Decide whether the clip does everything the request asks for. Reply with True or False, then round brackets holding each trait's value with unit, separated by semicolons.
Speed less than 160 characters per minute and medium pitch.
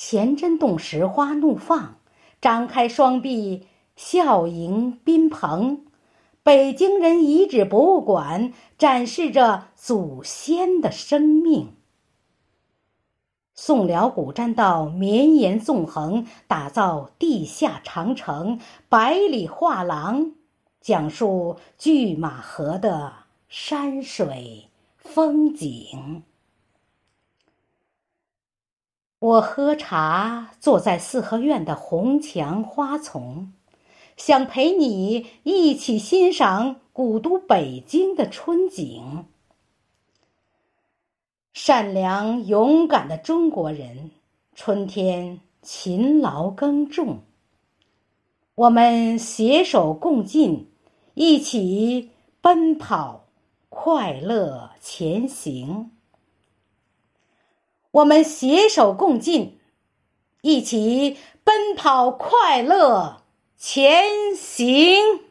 False (120 characters per minute; 245 Hz)